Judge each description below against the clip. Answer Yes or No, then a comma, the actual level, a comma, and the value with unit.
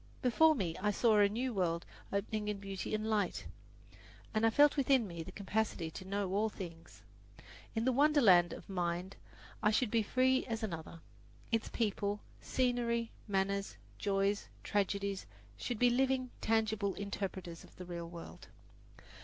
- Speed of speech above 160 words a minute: No, average, 155 wpm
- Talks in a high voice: Yes, high, 205 Hz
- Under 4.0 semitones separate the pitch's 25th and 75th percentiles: Yes, average, 3.5 semitones